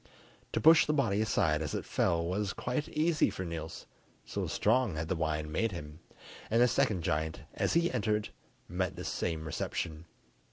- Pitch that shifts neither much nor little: No, wide, 6.2 semitones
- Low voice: Yes, very low, 90 Hz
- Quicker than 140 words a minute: Yes, average, 175 wpm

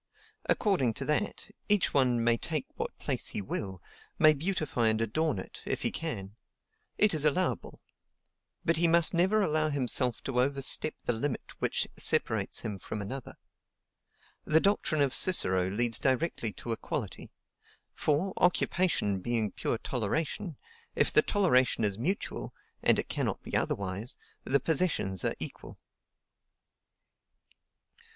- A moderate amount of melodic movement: No, wide, 6.5 semitones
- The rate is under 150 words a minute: Yes, slow, 135 wpm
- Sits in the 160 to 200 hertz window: No, low, 135 Hz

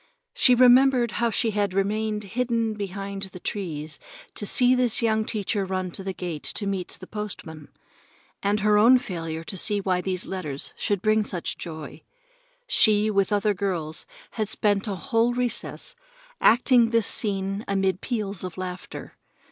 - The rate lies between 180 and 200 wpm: No, average, 155 wpm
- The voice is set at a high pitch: Yes, high, 205 Hz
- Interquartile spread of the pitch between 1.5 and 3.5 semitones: Yes, average, 2.9 semitones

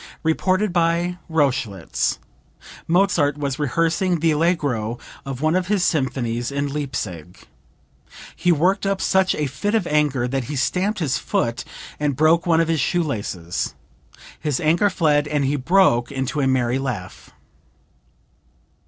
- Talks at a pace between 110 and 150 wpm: Yes, average, 145 wpm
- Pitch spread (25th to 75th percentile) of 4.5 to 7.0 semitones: Yes, average, 4.8 semitones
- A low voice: No, medium, 150 Hz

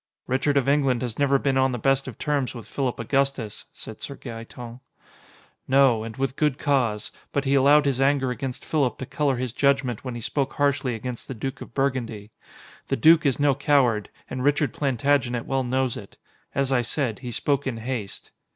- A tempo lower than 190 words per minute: No, average, 195 wpm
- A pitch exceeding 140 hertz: No, low, 130 Hz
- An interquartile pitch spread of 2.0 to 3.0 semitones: Yes, narrow, 2.5 semitones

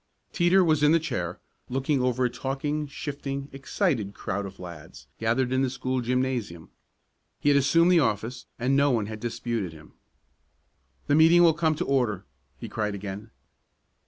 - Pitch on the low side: Yes, low, 130 Hz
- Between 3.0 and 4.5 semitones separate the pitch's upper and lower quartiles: No, average, 5.1 semitones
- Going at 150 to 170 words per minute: Yes, average, 165 wpm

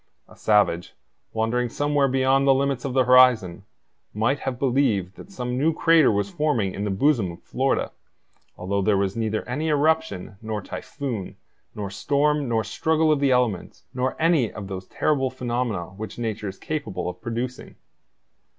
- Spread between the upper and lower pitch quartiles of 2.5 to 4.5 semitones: No, average, 5.3 semitones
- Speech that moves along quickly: No, average, 165 wpm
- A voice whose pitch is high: No, low, 125 Hz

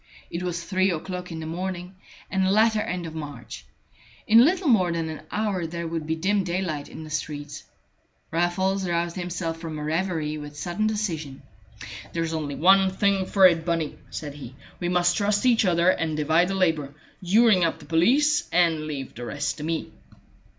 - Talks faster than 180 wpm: Yes, average, 190 wpm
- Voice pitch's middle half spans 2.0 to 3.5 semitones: Yes, average, 3.2 semitones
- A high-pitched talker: No, medium, 170 Hz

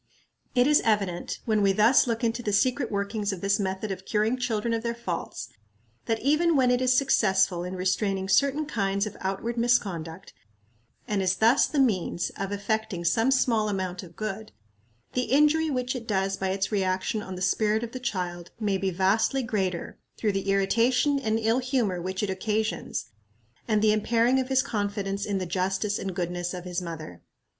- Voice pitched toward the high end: Yes, high, 210 Hz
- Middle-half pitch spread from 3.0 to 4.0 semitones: Yes, average, 3.7 semitones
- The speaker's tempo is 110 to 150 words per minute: No, average, 185 wpm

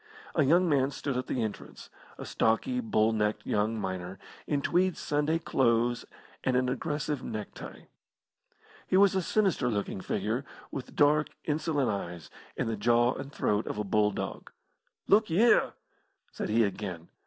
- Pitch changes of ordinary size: No, wide, 6.1 semitones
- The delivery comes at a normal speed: Yes, average, 155 wpm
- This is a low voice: Yes, low, 125 Hz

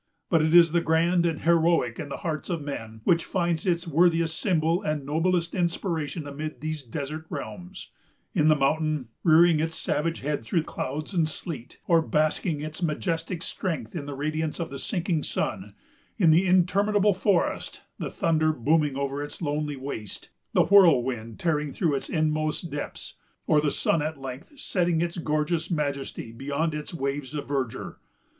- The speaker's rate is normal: Yes, average, 165 wpm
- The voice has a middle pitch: Yes, medium, 155 Hz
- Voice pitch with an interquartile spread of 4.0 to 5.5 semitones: No, average, 2.7 semitones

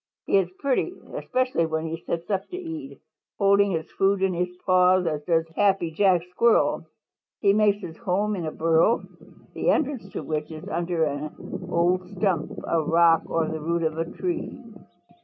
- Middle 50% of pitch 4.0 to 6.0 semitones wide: No, average, 3.5 semitones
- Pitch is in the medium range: Yes, medium, 180 Hz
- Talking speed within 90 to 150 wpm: No, average, 175 wpm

